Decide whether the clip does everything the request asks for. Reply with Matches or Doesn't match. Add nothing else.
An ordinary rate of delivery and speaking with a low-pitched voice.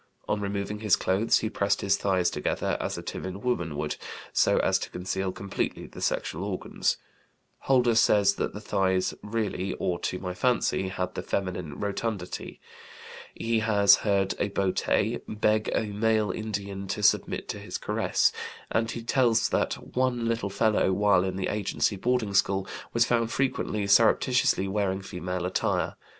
Matches